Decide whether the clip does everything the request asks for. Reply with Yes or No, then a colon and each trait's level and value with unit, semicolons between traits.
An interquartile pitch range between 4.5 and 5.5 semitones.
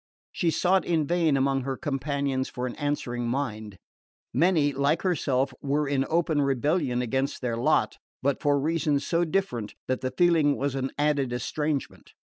No: average, 3.0 semitones